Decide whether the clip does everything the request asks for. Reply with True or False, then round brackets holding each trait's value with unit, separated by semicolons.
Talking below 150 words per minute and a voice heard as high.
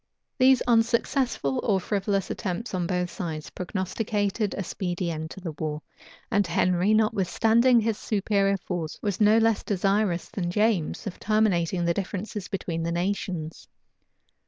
True (140 wpm; 195 Hz)